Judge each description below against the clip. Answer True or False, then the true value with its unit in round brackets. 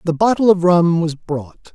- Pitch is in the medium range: True (175 Hz)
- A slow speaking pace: False (205 wpm)